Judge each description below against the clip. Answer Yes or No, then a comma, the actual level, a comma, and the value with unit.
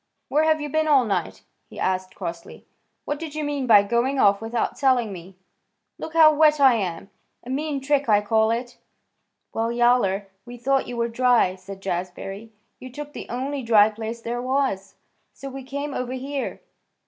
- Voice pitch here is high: Yes, high, 245 Hz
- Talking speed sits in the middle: Yes, average, 185 wpm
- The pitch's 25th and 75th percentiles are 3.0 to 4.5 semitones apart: No, average, 5.1 semitones